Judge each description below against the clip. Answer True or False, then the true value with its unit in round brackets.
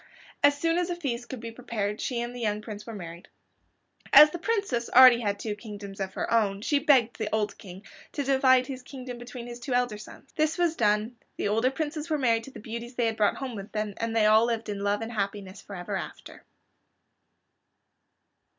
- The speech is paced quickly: True (215 wpm)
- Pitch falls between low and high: False (235 Hz)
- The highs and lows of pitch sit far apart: False (3.7 semitones)